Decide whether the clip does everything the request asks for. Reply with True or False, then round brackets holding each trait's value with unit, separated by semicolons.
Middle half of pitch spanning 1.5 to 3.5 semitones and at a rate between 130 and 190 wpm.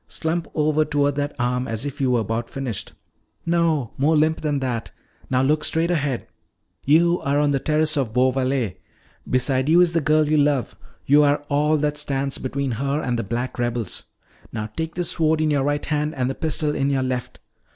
False (3.2 semitones; 200 wpm)